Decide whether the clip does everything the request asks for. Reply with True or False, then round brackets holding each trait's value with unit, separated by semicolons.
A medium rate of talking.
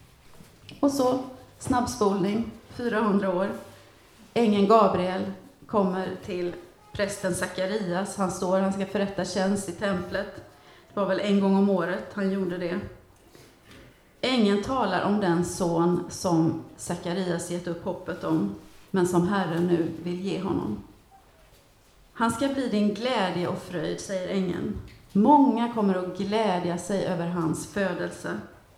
True (135 wpm)